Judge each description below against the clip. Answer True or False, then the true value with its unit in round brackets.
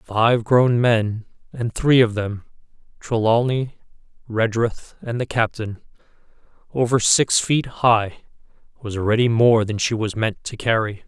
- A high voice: False (115 Hz)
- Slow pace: True (125 wpm)